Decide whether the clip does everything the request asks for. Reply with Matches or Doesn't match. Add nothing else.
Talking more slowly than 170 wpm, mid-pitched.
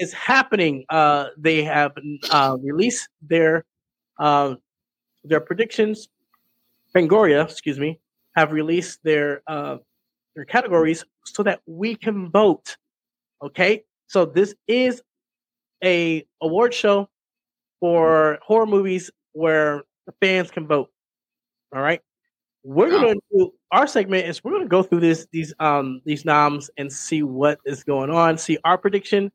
Matches